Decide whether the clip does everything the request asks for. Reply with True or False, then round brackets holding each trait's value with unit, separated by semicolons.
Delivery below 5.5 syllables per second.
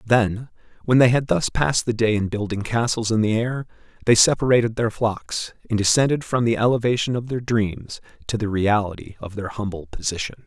True (5.3 syllables/s)